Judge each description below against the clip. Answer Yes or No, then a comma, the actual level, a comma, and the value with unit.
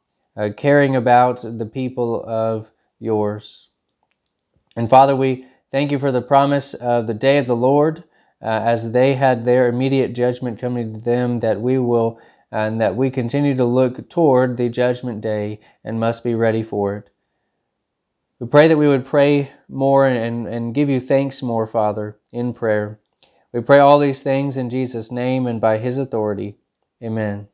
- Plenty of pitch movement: No, average, 3.0 semitones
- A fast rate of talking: No, average, 175 wpm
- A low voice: Yes, low, 125 Hz